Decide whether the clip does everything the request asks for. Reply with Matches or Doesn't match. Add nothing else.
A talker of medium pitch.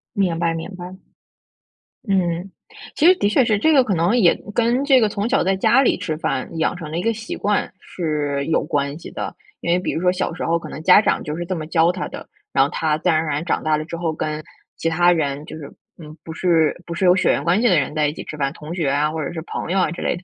Matches